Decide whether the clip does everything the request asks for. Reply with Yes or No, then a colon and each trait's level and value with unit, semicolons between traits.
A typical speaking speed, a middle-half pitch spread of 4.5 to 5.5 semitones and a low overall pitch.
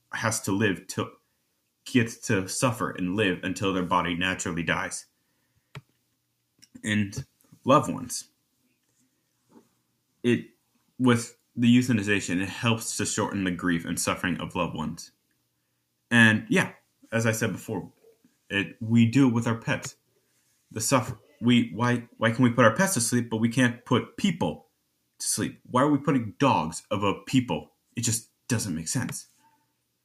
Yes: average, 150 wpm; average, 5.2 semitones; low, 115 Hz